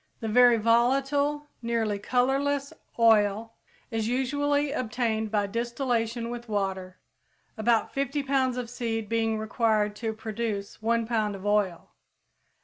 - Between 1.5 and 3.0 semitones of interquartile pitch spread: Yes, narrow, 2.6 semitones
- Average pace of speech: No, slow, 125 wpm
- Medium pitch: No, high, 230 Hz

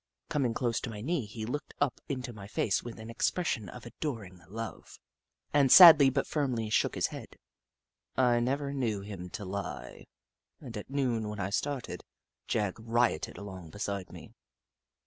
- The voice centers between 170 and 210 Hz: No, low, 115 Hz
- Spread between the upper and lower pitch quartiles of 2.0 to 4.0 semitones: No, average, 4.4 semitones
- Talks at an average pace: Yes, average, 165 wpm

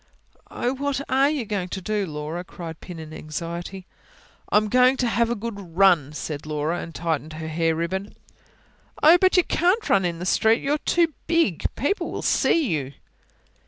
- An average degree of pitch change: No, wide, 7.6 semitones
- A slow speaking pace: No, average, 175 wpm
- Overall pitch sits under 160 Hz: No, high, 190 Hz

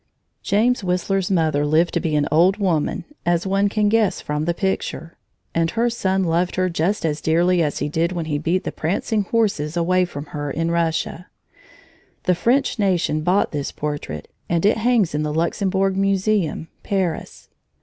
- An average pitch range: Yes, average, 3.5 semitones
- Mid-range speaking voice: Yes, medium, 175 Hz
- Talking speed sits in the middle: Yes, average, 175 wpm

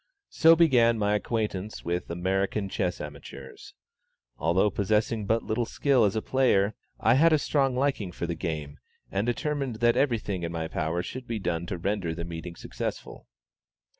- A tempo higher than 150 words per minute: Yes, average, 170 wpm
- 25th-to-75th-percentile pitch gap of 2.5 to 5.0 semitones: No, wide, 5.4 semitones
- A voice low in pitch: Yes, low, 105 Hz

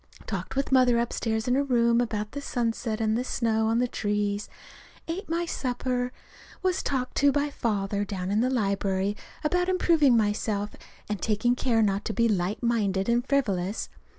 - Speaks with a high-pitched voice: Yes, high, 230 Hz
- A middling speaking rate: Yes, average, 175 wpm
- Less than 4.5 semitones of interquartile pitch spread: Yes, average, 3.7 semitones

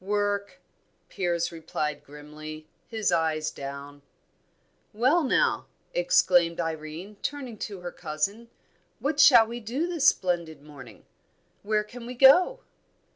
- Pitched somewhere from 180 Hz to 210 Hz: Yes, high, 190 Hz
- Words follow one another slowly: Yes, slow, 120 wpm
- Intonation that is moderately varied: No, wide, 7.6 semitones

